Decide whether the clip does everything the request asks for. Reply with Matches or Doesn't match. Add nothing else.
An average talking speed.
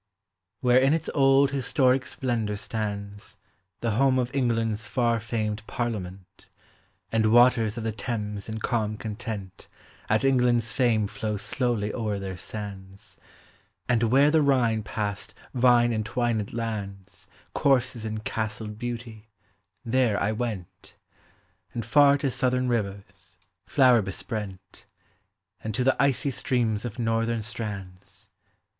Doesn't match